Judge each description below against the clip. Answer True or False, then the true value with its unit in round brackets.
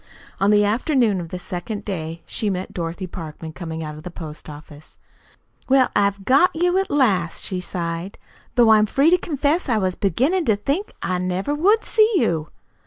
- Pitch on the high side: True (200 Hz)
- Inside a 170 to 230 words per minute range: True (185 wpm)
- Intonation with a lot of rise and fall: True (8.1 semitones)